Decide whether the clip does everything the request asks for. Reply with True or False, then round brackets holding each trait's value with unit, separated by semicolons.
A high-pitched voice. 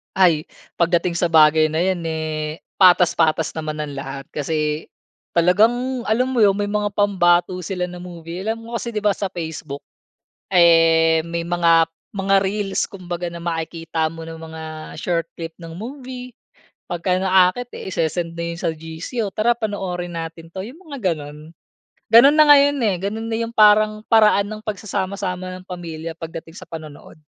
False (175 Hz)